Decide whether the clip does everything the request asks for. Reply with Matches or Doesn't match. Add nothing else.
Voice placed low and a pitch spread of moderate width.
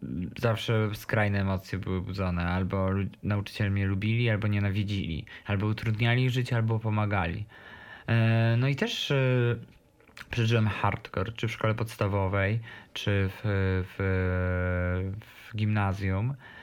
Matches